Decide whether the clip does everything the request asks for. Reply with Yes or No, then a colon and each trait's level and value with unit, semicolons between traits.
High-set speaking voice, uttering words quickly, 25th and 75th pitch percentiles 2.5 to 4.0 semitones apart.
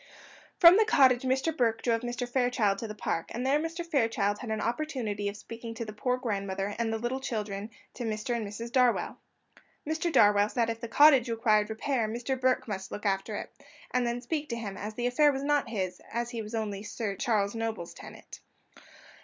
Yes: high, 230 Hz; fast, 210 wpm; average, 3.3 semitones